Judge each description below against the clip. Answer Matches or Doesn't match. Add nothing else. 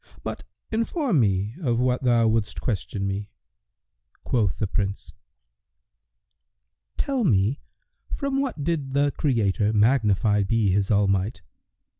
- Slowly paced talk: Matches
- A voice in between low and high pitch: Doesn't match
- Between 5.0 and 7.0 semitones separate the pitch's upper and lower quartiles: Matches